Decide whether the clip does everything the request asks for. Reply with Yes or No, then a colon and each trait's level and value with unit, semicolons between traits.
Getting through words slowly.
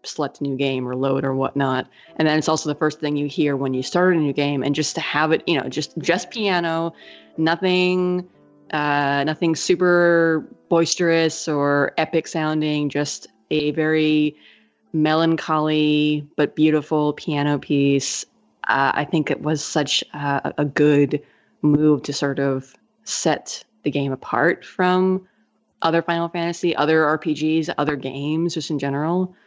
No: average, 155 wpm